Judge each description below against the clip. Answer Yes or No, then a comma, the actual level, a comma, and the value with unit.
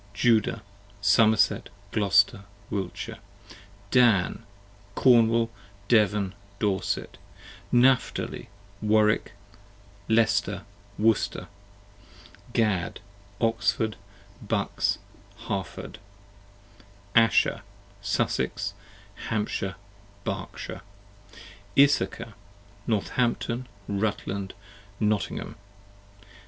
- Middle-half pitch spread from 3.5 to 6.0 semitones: No, narrow, 2.4 semitones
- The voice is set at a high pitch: No, low, 110 Hz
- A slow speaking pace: Yes, slow, 55 wpm